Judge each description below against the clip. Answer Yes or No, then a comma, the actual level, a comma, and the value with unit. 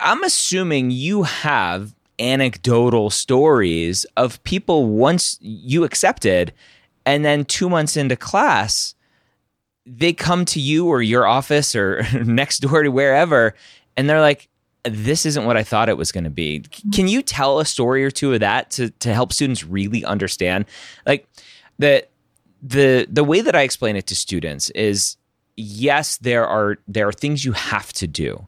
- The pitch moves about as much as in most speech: No, wide, 5.8 semitones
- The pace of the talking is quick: No, average, 165 wpm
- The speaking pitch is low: Yes, low, 125 Hz